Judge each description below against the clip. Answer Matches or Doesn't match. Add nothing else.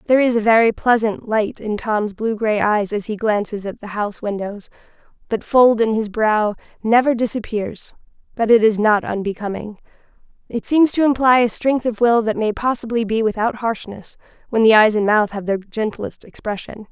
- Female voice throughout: Matches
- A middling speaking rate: Matches